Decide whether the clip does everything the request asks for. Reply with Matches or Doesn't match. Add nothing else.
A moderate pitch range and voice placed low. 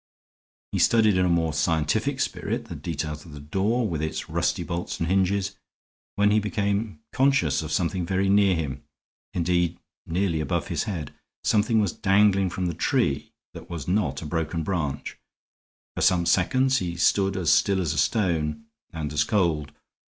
Matches